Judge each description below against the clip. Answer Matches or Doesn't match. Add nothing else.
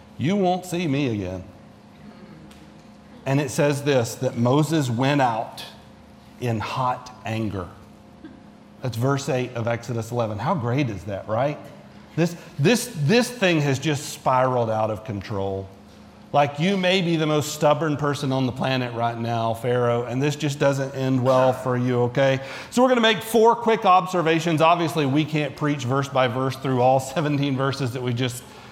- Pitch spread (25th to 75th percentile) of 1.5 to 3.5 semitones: Doesn't match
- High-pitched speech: Doesn't match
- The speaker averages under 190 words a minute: Matches